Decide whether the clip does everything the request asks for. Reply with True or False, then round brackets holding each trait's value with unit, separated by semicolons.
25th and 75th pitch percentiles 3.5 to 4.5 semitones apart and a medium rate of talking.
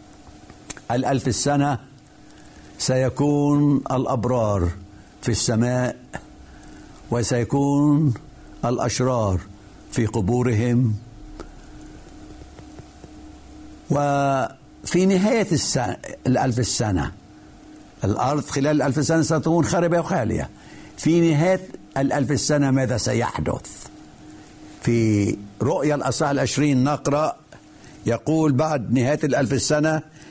True (4.2 semitones; 75 wpm)